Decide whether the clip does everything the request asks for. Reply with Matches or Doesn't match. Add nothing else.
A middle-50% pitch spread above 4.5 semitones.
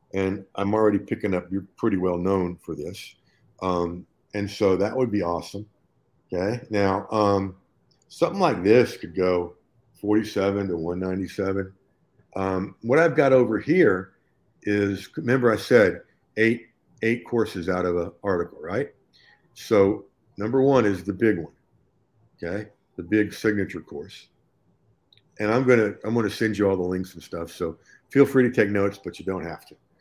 Doesn't match